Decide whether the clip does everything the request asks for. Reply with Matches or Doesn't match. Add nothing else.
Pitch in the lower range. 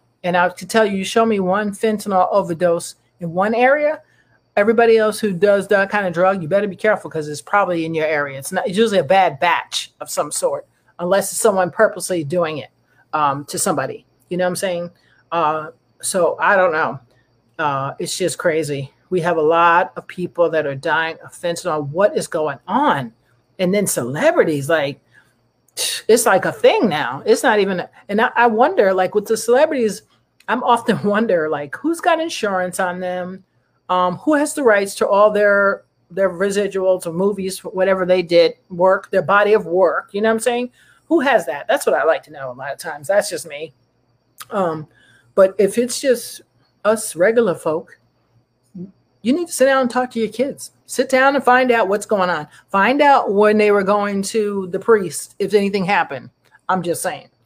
Doesn't match